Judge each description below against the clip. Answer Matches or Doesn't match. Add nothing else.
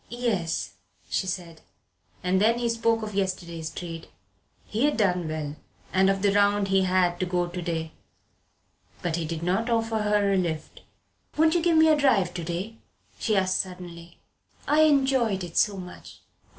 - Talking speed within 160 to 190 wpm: Matches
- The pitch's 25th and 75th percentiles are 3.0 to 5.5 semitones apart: Matches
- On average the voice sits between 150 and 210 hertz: Matches